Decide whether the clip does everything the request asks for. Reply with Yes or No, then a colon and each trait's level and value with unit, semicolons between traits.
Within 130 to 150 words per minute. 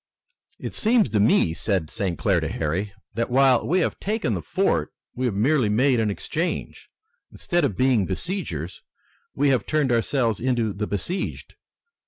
No: average, 165 wpm